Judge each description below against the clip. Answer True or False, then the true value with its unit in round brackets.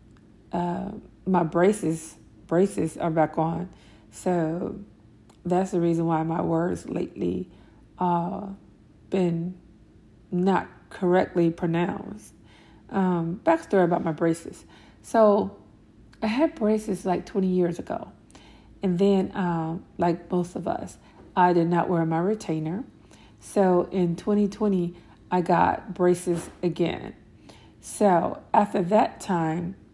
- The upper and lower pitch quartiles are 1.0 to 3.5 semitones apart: True (2.7 semitones)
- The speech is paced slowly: True (115 wpm)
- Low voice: False (175 Hz)